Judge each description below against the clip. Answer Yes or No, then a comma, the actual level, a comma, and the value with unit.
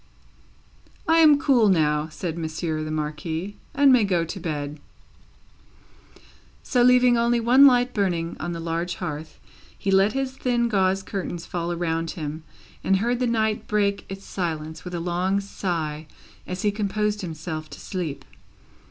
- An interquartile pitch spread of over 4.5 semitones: Yes, average, 5.1 semitones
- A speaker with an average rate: Yes, average, 155 wpm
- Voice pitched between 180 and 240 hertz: Yes, medium, 185 Hz